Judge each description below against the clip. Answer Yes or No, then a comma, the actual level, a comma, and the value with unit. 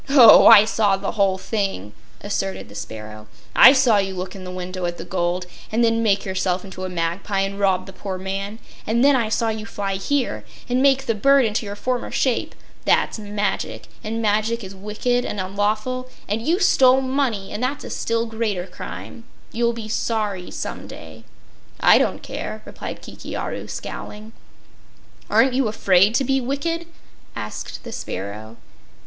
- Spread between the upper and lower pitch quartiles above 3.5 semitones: Yes, average, 4.0 semitones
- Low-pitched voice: No, high, 210 Hz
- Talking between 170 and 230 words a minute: Yes, average, 175 wpm